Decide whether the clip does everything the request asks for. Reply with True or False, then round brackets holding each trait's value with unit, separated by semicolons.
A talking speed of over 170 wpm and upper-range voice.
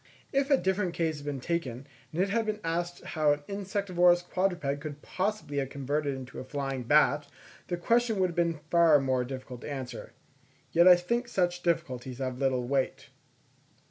False (185 wpm; 165 Hz)